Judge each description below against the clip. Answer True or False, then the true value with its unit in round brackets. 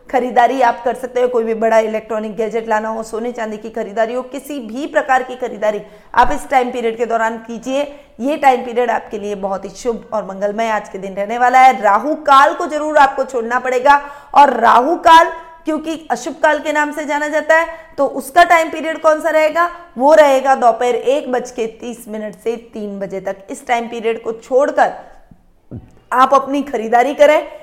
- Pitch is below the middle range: False (250 Hz)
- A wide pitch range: False (4.4 semitones)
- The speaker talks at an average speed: False (200 wpm)